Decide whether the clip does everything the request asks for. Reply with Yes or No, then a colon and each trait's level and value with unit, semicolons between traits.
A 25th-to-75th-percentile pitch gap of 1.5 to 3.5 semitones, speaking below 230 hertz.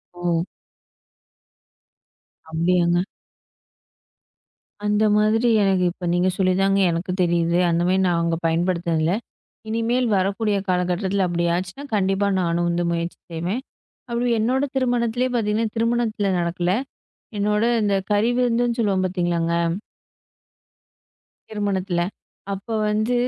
No: average, 4.0 semitones; high, 190 Hz